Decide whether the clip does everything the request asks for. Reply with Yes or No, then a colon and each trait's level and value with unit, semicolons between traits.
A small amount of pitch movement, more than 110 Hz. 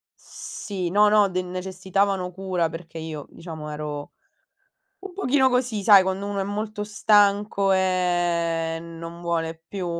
No: average, 3.3 semitones; medium, 185 Hz